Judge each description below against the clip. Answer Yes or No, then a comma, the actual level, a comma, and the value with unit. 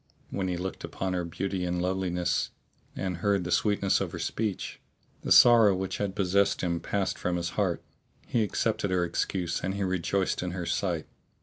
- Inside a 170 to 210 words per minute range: Yes, average, 185 wpm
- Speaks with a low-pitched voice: Yes, very low, 95 Hz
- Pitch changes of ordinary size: No, narrow, 1.9 semitones